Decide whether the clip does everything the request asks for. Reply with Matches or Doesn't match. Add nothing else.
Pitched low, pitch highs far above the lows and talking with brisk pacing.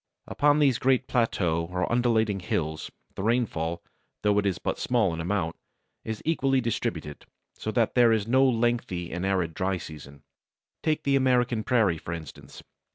Doesn't match